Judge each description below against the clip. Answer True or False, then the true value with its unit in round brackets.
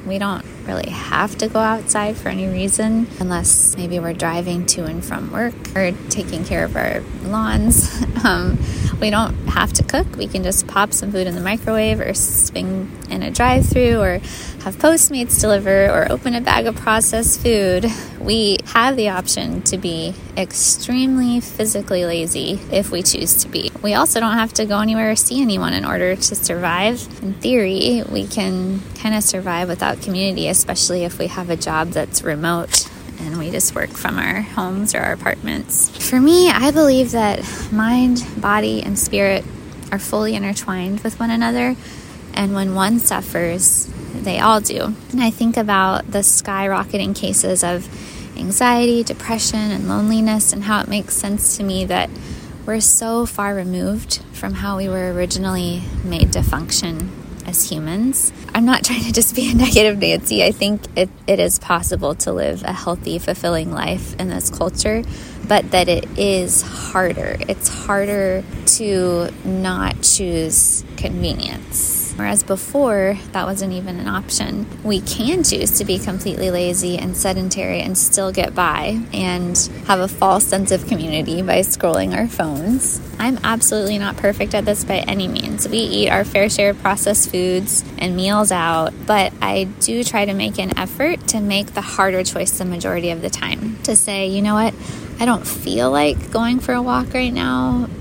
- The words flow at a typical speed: True (175 wpm)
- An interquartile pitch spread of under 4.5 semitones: True (3.3 semitones)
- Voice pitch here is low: False (200 Hz)